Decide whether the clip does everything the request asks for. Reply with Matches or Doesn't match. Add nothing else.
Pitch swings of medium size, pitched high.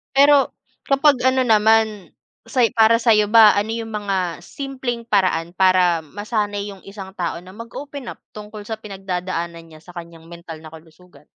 Matches